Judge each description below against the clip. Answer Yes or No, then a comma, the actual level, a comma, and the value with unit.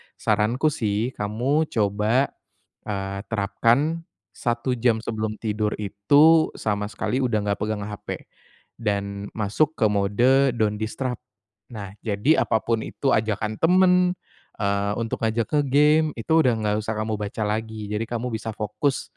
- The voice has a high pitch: No, low, 110 Hz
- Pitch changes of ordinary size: Yes, average, 3.5 semitones